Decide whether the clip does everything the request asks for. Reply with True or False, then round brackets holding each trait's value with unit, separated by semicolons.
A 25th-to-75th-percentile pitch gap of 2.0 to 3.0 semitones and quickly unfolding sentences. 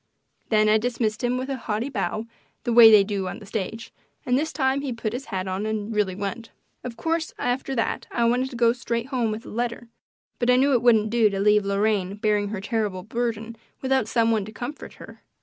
True (2.7 semitones; 225 wpm)